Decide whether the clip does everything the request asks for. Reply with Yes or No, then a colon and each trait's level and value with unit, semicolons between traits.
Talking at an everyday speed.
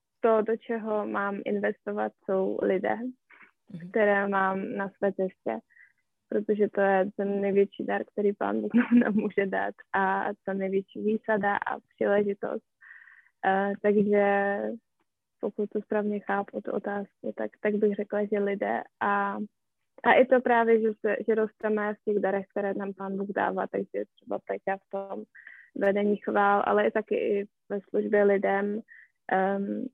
Yes: average, 150 wpm